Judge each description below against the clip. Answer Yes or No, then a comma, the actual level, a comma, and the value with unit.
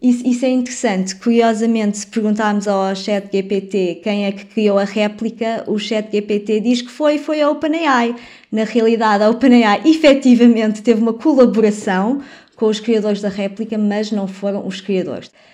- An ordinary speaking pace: Yes, average, 165 wpm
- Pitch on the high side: Yes, high, 220 Hz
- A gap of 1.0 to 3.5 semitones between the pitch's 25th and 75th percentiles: Yes, average, 2.9 semitones